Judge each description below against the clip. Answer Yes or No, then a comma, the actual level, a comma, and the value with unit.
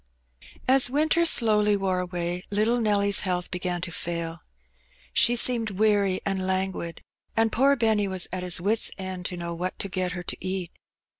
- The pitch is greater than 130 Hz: Yes, high, 190 Hz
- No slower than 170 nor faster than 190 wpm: Yes, average, 175 wpm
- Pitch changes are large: No, average, 3.3 semitones